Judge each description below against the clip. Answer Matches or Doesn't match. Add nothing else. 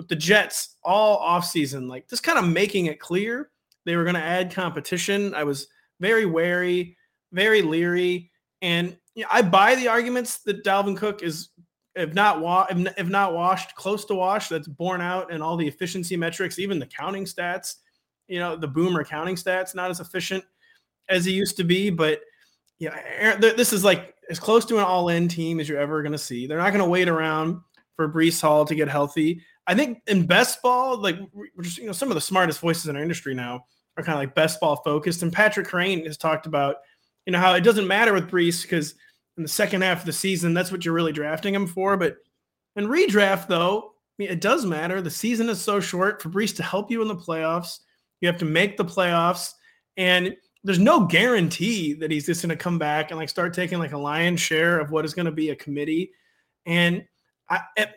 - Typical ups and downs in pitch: Matches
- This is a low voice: Doesn't match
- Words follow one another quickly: Matches